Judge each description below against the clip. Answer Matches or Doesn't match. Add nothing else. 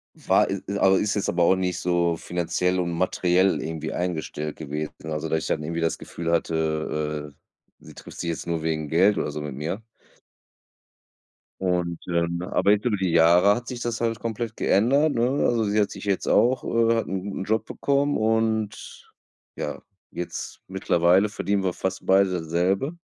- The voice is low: Matches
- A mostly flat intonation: Doesn't match